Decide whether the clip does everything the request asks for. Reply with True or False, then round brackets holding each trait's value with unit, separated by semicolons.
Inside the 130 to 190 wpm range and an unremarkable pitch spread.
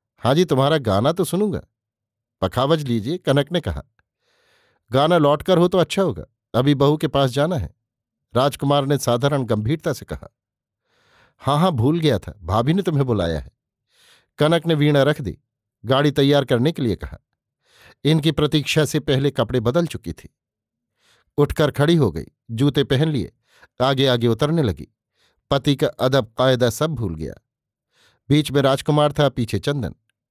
True (160 wpm; 4.3 semitones)